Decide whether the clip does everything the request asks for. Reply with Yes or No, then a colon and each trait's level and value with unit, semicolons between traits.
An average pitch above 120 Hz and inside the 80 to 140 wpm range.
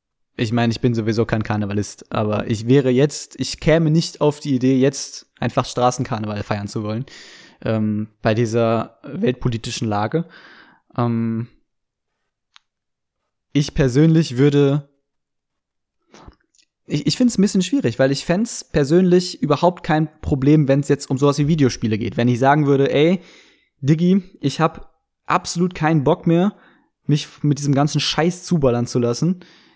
No: medium, 140 Hz; average, 150 wpm